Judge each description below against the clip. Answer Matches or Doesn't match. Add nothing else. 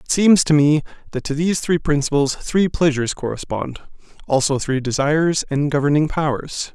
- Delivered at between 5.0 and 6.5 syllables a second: Matches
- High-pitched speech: Doesn't match